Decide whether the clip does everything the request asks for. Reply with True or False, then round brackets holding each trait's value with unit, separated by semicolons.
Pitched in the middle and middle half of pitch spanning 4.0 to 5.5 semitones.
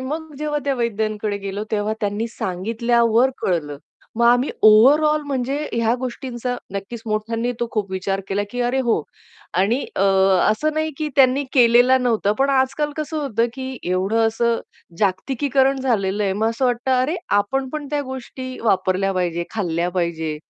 False (235 Hz; 4.4 semitones)